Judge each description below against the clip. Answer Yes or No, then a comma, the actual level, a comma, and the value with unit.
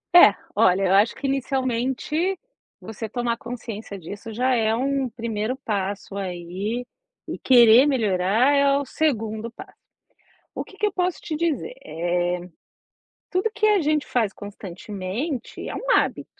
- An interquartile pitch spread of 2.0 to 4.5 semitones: No, wide, 5.6 semitones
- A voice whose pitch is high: Yes, high, 235 Hz